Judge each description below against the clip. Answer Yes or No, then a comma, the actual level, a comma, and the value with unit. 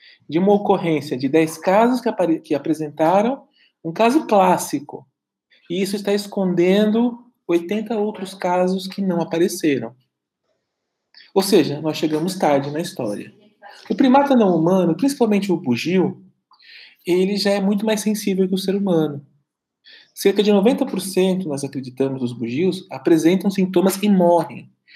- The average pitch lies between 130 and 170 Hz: No, medium, 185 Hz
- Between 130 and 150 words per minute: Yes, average, 140 wpm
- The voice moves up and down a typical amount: Yes, average, 4.0 semitones